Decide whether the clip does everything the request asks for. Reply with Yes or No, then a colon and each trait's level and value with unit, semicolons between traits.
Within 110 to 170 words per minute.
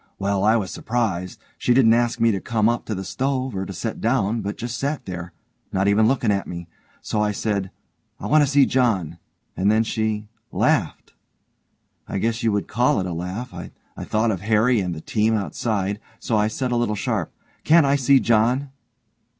No: average, 200 wpm